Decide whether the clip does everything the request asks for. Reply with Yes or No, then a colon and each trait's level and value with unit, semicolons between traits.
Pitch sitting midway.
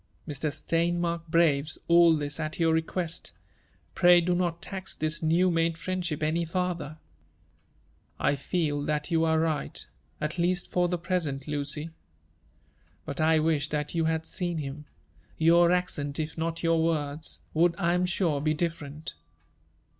Yes: medium, 165 Hz